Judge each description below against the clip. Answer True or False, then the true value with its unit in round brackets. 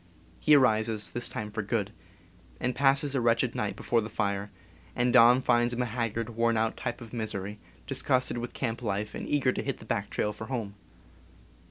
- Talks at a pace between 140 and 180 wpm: False (190 wpm)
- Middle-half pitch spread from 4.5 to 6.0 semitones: False (2.5 semitones)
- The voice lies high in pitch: False (115 Hz)